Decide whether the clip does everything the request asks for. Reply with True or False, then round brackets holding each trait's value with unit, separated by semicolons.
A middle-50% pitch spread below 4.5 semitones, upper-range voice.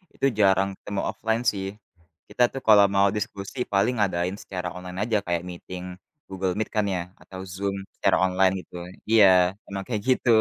False (2.4 semitones; 100 Hz)